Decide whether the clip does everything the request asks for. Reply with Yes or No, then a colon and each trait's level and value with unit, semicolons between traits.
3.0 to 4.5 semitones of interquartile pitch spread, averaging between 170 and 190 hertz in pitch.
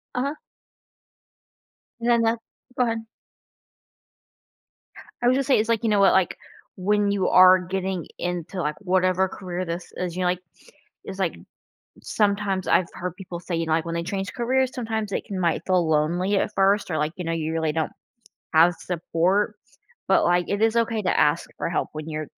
Yes: average, 3.5 semitones; medium, 185 Hz